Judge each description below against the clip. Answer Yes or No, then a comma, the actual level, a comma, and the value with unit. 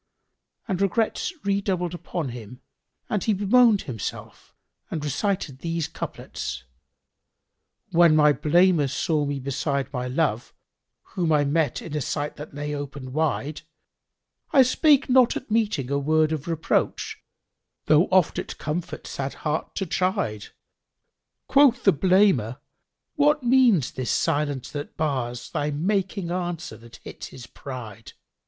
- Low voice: No, medium, 155 Hz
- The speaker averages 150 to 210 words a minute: No, average, 140 wpm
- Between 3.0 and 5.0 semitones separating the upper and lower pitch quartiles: No, wide, 5.4 semitones